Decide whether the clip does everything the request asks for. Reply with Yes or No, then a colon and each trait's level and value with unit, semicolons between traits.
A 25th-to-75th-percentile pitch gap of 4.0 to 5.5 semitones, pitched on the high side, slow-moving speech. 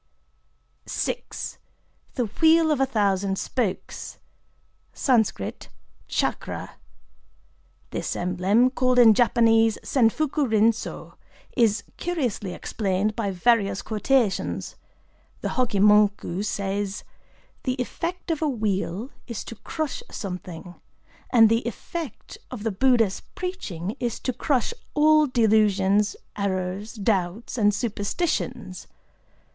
Yes: average, 4.3 semitones; high, 220 Hz; slow, 105 wpm